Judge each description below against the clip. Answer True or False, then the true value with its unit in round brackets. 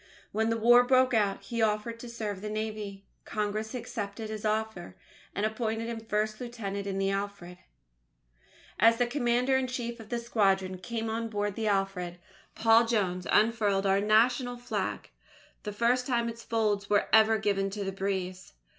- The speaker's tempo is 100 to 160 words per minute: False (170 wpm)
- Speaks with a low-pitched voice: False (215 Hz)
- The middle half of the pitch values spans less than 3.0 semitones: True (2.6 semitones)